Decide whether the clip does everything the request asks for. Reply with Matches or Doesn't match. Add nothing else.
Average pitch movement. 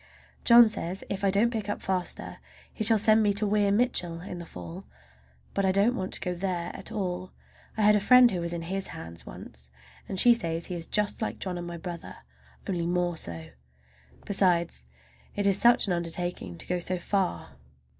Matches